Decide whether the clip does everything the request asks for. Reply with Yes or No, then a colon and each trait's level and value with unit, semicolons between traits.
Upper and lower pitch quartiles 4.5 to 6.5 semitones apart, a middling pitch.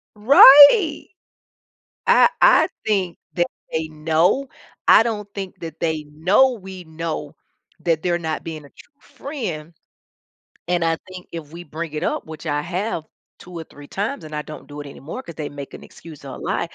Yes: average, 4.8 semitones; medium, 170 Hz